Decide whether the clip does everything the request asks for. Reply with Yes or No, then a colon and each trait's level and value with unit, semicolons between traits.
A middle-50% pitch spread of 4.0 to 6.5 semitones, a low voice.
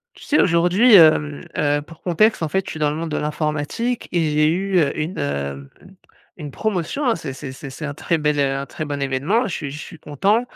No: average, 4.3 semitones; medium, 155 Hz